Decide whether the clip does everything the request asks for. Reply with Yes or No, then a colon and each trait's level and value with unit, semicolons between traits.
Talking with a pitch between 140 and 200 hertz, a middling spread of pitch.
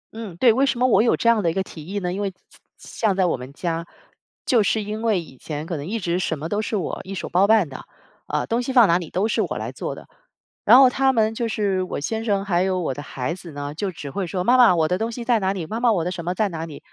Yes: high, 190 Hz; average, 4.9 semitones